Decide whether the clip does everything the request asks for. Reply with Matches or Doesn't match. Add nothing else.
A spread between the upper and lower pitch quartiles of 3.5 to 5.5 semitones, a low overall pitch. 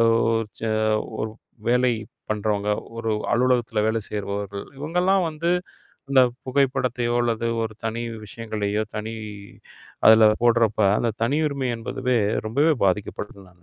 Doesn't match